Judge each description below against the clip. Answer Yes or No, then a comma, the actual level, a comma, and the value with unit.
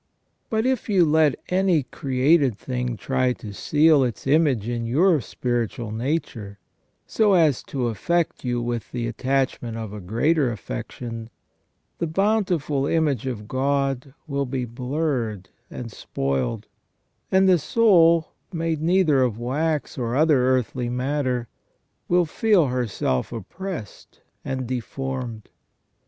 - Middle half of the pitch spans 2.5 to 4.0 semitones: No, average, 5.2 semitones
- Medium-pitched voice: No, low, 130 Hz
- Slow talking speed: Yes, slow, 125 wpm